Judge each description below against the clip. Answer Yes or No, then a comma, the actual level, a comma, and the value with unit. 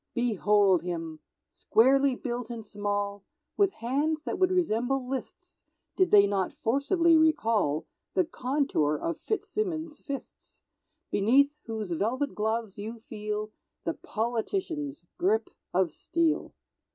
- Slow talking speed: Yes, slow, 115 wpm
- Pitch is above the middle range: Yes, high, 240 Hz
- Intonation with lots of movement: Yes, wide, 6.5 semitones